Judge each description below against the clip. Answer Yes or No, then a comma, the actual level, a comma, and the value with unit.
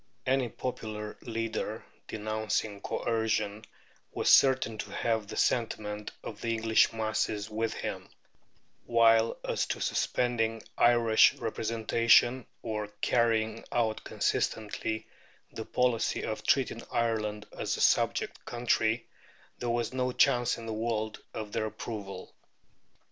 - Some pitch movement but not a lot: No, narrow, 1.3 semitones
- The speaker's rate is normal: No, slow, 120 wpm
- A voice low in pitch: Yes, low, 110 Hz